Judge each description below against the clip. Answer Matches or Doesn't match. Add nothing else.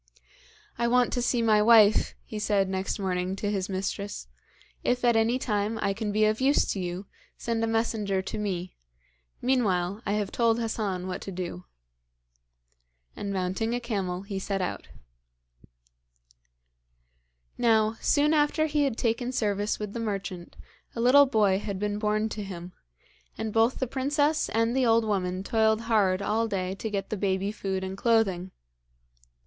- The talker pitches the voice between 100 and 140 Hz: Doesn't match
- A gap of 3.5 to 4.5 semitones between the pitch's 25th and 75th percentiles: Doesn't match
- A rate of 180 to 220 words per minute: Doesn't match